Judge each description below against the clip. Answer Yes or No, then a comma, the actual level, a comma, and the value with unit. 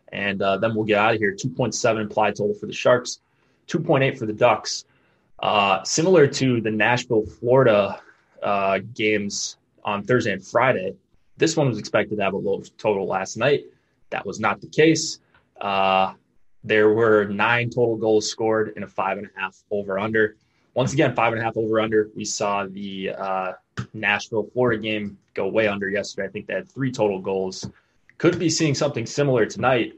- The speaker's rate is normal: Yes, average, 185 wpm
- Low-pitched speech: Yes, low, 110 Hz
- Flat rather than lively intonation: No, average, 3.2 semitones